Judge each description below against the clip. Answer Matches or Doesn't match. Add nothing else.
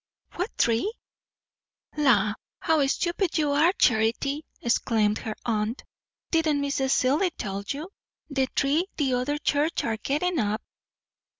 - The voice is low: Doesn't match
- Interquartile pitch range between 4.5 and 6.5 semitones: Matches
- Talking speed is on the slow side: Matches